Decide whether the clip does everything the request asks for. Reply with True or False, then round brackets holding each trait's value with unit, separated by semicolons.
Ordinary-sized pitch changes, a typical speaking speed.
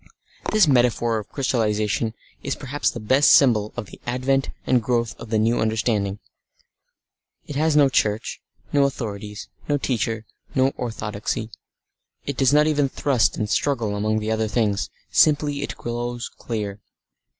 True (4.0 semitones; 150 wpm)